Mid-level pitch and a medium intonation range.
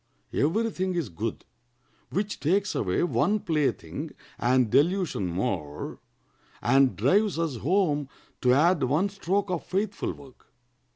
No: medium, 160 Hz; wide, 7.1 semitones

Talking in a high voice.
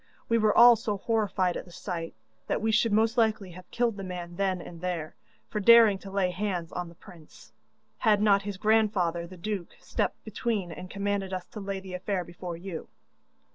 Yes: high, 195 Hz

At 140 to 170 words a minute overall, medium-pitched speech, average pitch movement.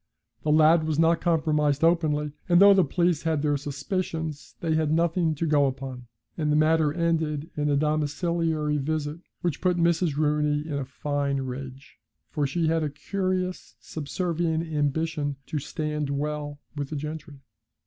No: average, 160 wpm; medium, 155 Hz; narrow, 2.1 semitones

